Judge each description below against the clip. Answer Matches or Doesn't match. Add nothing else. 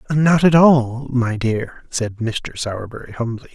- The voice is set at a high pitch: Doesn't match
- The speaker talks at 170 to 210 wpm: Doesn't match